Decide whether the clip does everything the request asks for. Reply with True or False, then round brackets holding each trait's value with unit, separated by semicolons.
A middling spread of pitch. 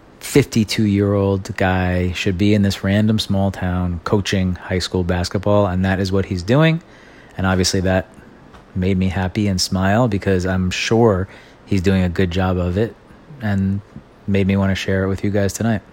False (1.9 semitones)